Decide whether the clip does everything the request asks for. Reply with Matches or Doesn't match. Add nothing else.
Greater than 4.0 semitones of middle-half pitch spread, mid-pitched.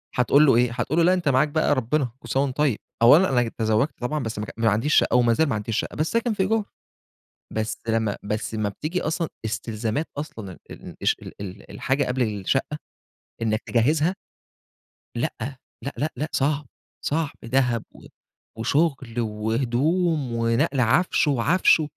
Doesn't match